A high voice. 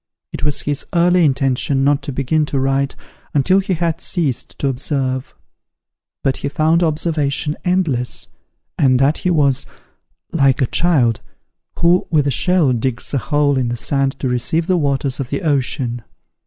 No: medium, 140 Hz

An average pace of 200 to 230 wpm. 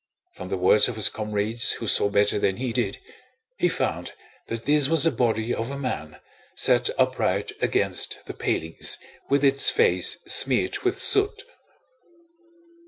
No: average, 155 wpm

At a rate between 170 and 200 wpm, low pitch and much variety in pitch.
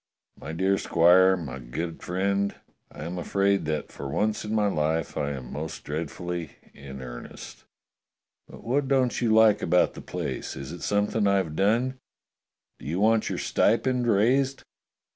No: average, 160 wpm; very low, 95 Hz; wide, 5.7 semitones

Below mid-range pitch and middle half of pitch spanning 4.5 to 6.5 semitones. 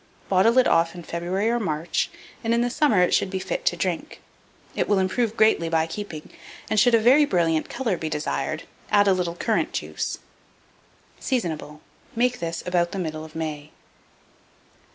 No: medium, 185 Hz; wide, 5.6 semitones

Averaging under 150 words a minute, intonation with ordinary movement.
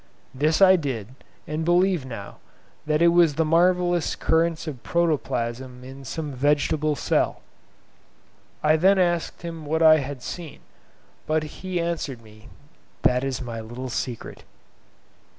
Yes: slow, 135 wpm; average, 4.6 semitones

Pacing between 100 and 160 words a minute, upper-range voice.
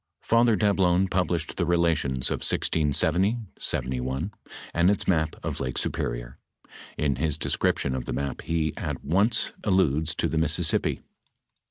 No: average, 140 wpm; very low, 80 Hz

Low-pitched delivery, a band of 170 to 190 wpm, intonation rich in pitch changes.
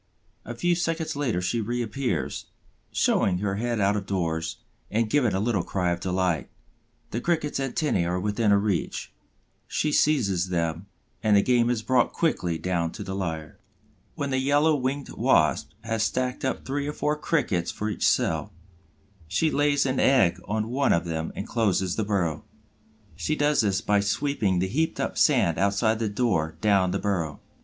Yes: low, 105 Hz; average, 175 wpm; wide, 6.3 semitones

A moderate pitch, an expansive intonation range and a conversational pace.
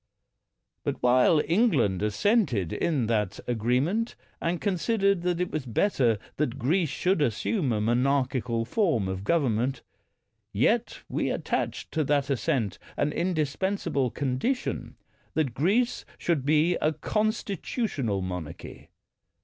No: medium, 145 Hz; wide, 7.2 semitones; slow, 120 wpm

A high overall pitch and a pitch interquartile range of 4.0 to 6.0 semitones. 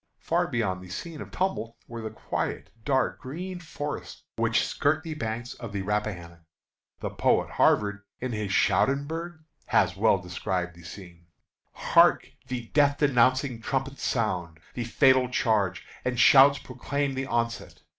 No: low, 120 Hz; wide, 5.4 semitones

